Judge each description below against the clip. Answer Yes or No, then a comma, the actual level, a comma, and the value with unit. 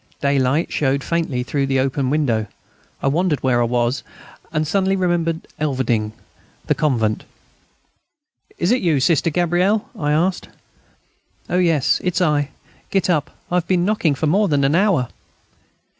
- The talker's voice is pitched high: No, medium, 155 Hz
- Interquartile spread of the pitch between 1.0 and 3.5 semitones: No, average, 4.7 semitones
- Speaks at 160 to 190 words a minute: No, average, 150 wpm